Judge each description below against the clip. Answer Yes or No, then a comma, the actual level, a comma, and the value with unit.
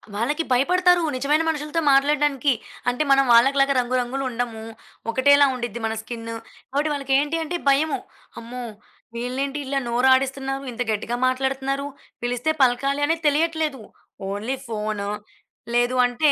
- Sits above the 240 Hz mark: Yes, very high, 270 Hz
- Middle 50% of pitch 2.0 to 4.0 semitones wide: Yes, average, 3.1 semitones